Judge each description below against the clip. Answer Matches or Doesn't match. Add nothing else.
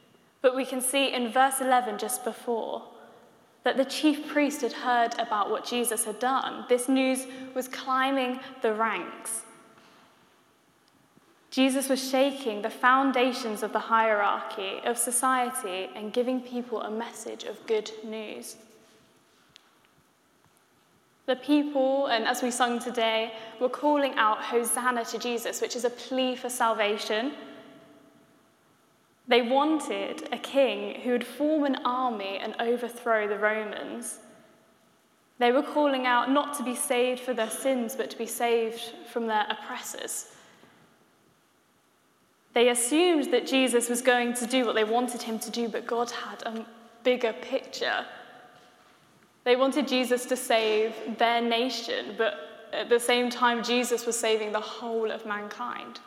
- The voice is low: Doesn't match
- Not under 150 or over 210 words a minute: Doesn't match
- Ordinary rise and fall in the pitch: Doesn't match